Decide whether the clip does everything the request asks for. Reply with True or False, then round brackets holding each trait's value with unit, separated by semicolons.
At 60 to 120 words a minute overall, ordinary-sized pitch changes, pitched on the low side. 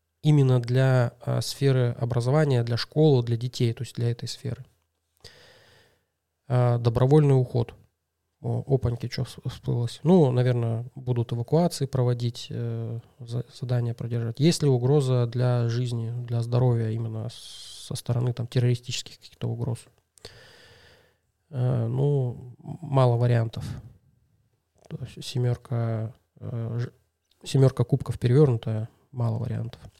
False (115 wpm; 1.9 semitones; 120 Hz)